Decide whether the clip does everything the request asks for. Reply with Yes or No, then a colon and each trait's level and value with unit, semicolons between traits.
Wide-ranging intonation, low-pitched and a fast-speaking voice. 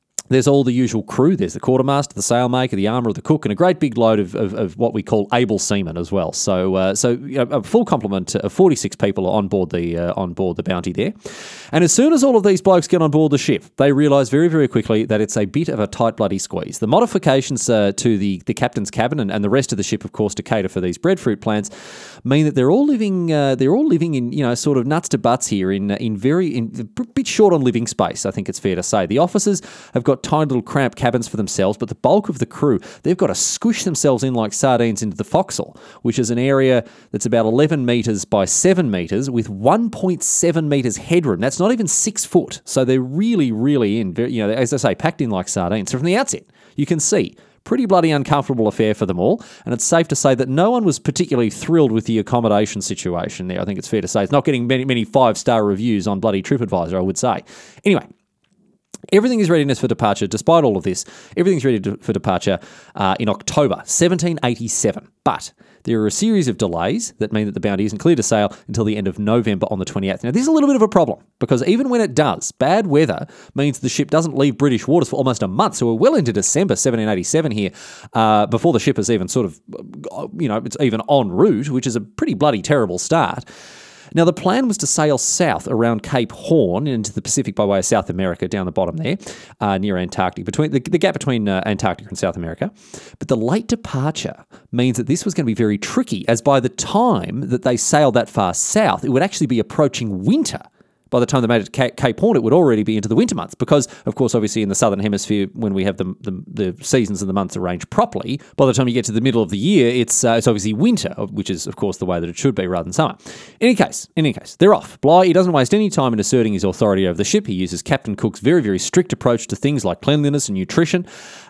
Yes: wide, 6.6 semitones; low, 125 Hz; fast, 250 wpm